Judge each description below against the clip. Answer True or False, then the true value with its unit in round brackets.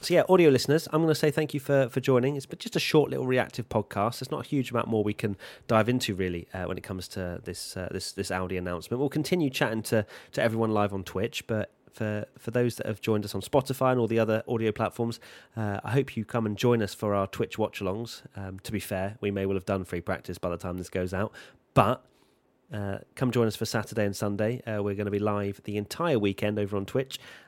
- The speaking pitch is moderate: False (110 Hz)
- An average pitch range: True (4.2 semitones)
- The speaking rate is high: True (260 wpm)